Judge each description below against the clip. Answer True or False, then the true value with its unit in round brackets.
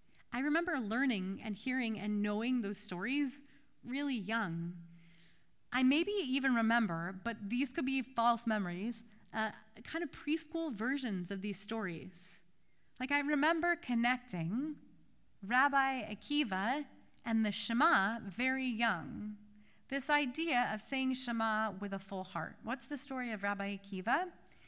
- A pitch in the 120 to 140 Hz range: False (235 Hz)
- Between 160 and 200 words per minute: False (135 wpm)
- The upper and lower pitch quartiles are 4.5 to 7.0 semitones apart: True (4.8 semitones)